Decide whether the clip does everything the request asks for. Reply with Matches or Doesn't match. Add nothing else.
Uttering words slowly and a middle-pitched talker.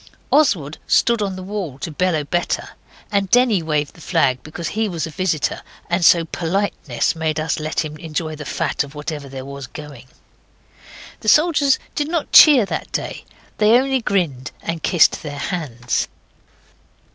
Doesn't match